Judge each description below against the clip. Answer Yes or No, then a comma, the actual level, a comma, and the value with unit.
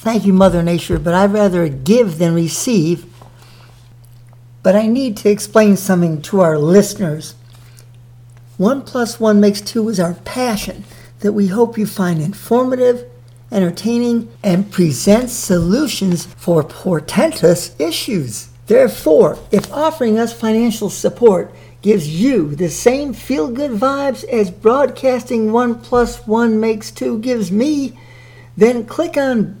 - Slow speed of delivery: Yes, slow, 130 wpm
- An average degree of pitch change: No, wide, 6.2 semitones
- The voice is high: Yes, high, 200 Hz